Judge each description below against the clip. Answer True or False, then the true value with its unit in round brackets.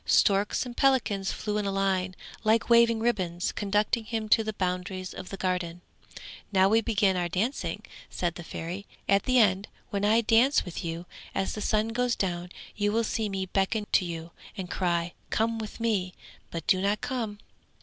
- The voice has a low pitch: False (200 Hz)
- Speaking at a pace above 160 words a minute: True (185 wpm)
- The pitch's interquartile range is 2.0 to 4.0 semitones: True (3.4 semitones)